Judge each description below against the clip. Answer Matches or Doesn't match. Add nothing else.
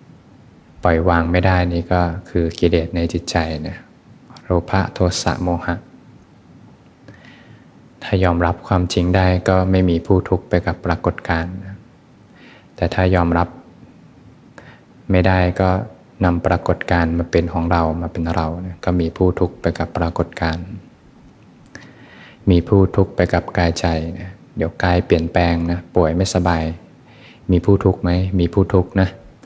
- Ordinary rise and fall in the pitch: Doesn't match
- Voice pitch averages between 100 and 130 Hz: Doesn't match